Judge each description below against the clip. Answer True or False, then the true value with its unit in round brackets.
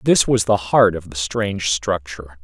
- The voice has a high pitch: False (90 Hz)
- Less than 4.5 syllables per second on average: False (4.8 syllables/s)